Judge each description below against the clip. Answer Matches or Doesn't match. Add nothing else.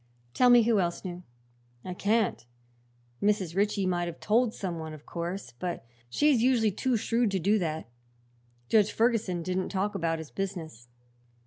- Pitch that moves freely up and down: Doesn't match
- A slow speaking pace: Doesn't match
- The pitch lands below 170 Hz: Doesn't match